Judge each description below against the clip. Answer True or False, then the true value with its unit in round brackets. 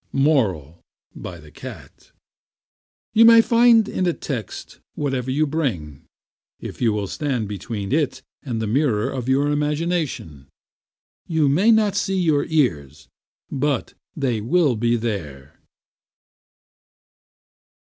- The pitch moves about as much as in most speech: False (7.2 semitones)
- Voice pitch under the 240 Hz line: True (135 Hz)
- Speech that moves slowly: True (120 wpm)